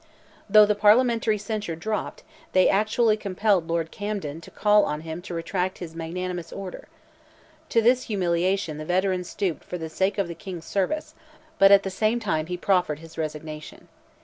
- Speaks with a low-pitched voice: No, medium, 185 Hz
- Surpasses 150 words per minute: Yes, average, 175 wpm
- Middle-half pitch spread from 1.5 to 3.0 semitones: No, average, 4.0 semitones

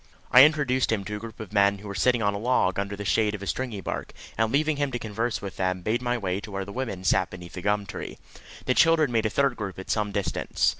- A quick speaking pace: Yes, fast, 265 wpm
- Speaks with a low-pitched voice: Yes, low, 105 Hz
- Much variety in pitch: No, average, 3.7 semitones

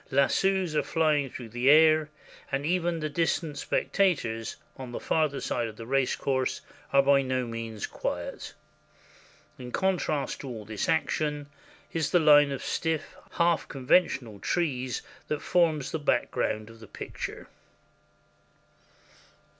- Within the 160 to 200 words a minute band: No, average, 140 wpm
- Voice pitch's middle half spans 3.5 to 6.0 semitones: Yes, average, 4.3 semitones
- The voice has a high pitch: No, medium, 140 Hz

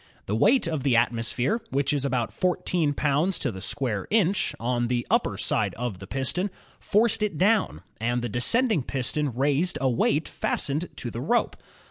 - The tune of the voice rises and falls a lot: Yes, wide, 6.8 semitones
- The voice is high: No, medium, 140 Hz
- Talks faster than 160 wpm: Yes, average, 175 wpm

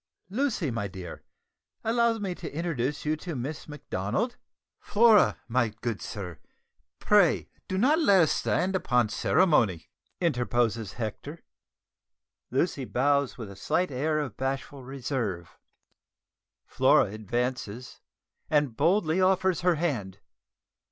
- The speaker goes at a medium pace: No, slow, 120 wpm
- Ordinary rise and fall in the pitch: No, wide, 7.3 semitones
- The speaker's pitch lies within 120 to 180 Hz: Yes, medium, 140 Hz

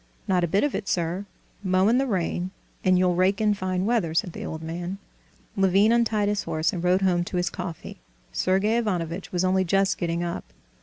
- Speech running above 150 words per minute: Yes, fast, 205 wpm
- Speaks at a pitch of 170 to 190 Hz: Yes, medium, 185 Hz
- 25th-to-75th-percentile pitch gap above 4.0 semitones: No, narrow, 2.4 semitones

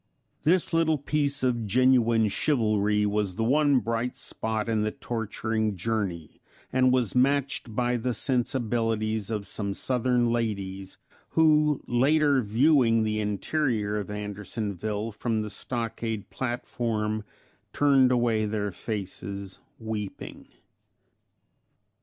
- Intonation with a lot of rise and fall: No, average, 3.3 semitones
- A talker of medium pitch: No, low, 115 Hz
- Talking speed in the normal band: No, slow, 110 wpm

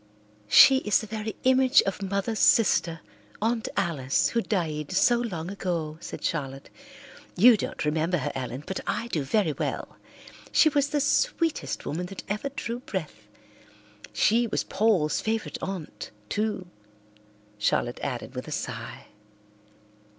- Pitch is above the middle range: Yes, high, 200 Hz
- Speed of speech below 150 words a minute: Yes, average, 140 wpm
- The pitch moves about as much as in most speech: No, wide, 6.4 semitones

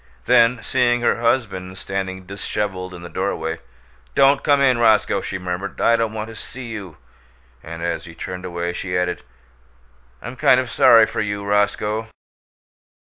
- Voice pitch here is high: No, low, 105 Hz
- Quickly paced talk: No, average, 160 wpm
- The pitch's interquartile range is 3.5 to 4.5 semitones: Yes, average, 4.1 semitones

